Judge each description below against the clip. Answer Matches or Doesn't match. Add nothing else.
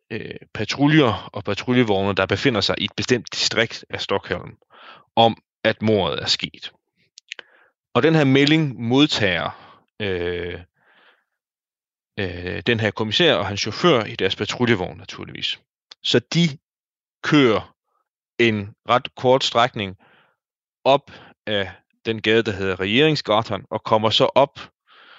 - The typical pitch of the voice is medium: Doesn't match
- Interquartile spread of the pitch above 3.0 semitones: Matches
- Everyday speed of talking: Doesn't match